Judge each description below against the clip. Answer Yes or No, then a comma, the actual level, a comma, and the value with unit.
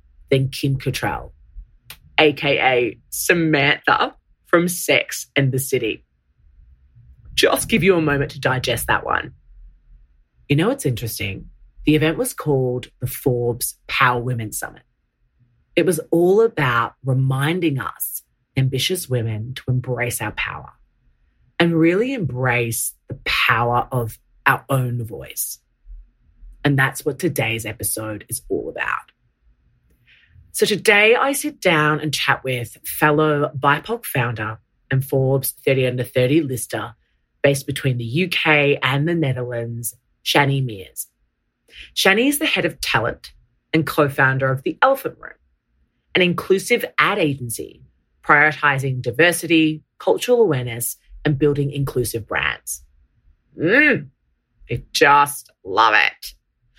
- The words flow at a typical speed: No, slow, 125 wpm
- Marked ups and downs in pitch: No, average, 4.7 semitones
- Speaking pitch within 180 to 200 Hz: No, low, 135 Hz